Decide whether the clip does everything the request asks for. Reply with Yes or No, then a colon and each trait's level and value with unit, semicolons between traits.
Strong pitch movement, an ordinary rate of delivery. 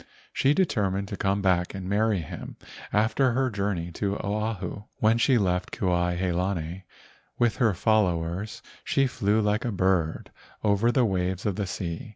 No: average, 3.2 semitones; average, 165 wpm